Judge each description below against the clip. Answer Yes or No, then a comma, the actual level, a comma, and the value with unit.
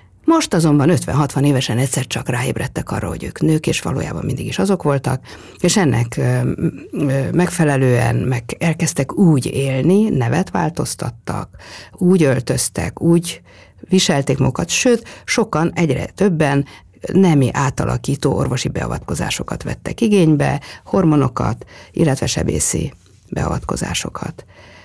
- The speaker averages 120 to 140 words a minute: No, average, 110 wpm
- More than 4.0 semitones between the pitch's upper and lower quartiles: Yes, average, 5.1 semitones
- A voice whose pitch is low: No, medium, 150 Hz